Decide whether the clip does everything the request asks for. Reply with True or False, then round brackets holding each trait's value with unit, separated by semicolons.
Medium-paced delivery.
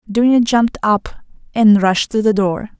True (170 wpm)